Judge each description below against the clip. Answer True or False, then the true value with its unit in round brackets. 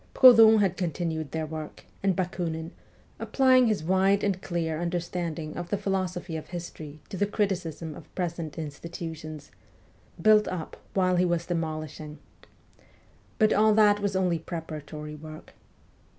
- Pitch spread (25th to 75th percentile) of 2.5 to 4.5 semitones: True (3.4 semitones)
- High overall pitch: False (175 Hz)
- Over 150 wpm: False (140 wpm)